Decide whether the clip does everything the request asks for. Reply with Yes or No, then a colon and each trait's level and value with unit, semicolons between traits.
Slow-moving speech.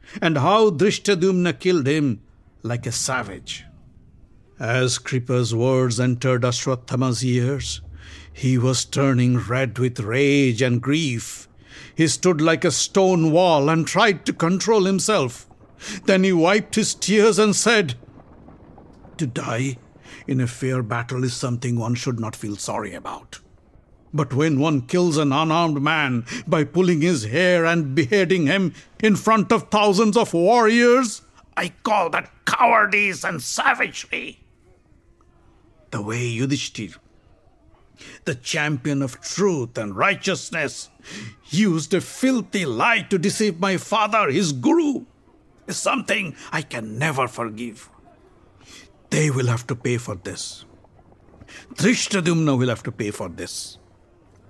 Yes: slow, 130 wpm